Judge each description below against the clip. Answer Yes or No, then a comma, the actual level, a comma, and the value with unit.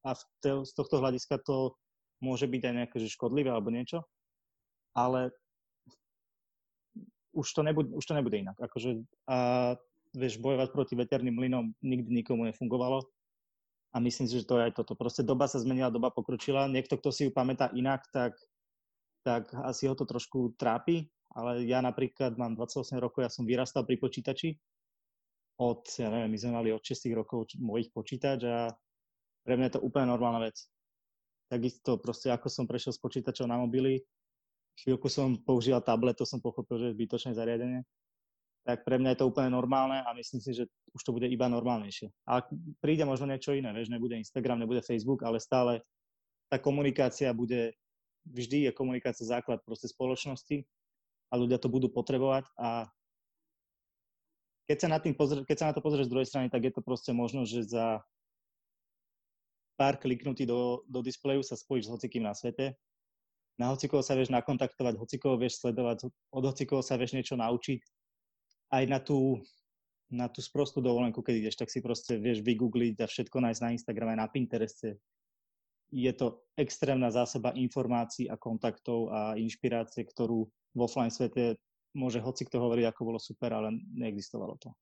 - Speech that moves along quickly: Yes, fast, 170 wpm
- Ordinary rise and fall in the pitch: No, narrow, 2.0 semitones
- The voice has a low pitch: Yes, low, 125 Hz